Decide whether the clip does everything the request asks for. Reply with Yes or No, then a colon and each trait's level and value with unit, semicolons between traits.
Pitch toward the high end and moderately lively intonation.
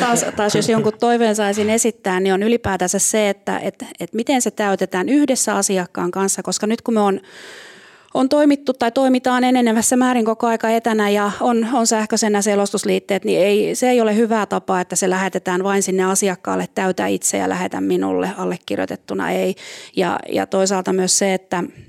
Yes: high, 205 Hz; average, 3.4 semitones